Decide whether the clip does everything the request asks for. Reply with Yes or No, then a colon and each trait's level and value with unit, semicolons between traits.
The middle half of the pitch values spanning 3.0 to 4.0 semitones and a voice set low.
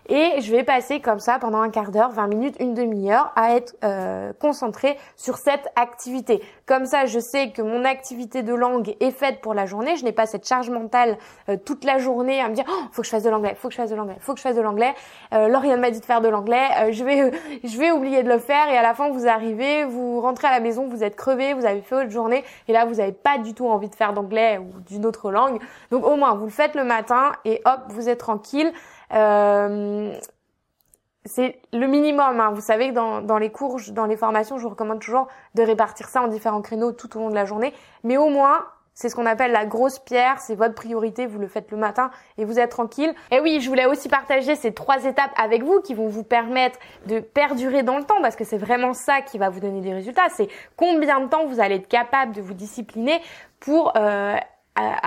No: average, 3.4 semitones; high, 240 Hz